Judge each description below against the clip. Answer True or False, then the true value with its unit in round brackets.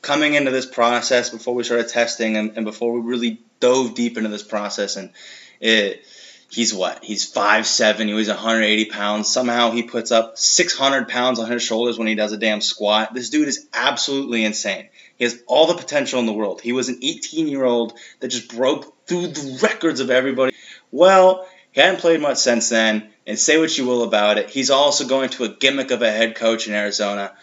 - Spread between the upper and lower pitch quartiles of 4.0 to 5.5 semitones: False (3.5 semitones)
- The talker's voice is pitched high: False (120 Hz)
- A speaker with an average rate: False (210 wpm)